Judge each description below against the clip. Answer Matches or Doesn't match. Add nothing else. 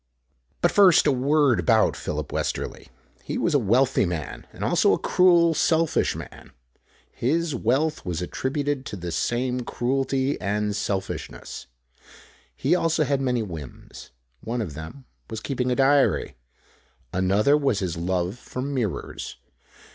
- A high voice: Doesn't match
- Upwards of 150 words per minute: Doesn't match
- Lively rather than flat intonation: Matches